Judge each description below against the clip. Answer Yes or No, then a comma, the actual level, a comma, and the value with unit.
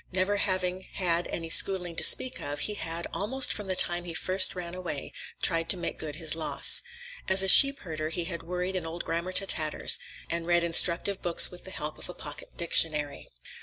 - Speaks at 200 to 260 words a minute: Yes, fast, 205 wpm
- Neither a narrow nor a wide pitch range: No, narrow, 2.2 semitones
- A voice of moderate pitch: Yes, medium, 175 Hz